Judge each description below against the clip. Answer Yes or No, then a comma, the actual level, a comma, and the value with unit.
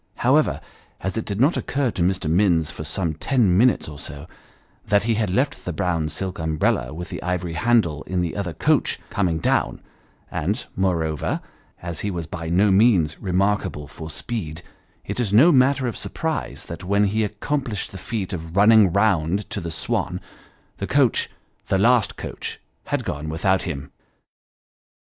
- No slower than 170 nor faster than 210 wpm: Yes, average, 180 wpm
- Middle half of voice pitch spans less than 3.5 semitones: No, average, 4.6 semitones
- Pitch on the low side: Yes, very low, 95 Hz